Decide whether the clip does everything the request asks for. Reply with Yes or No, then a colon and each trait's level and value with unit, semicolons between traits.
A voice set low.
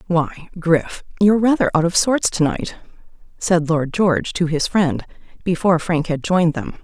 No: medium, 170 Hz